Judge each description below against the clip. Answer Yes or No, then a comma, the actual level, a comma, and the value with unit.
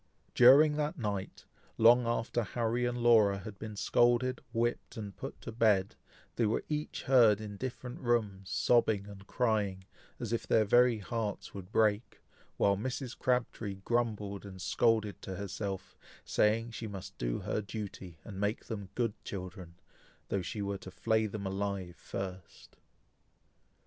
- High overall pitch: No, low, 110 Hz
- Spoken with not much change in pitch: No, average, 3.2 semitones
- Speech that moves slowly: No, average, 150 wpm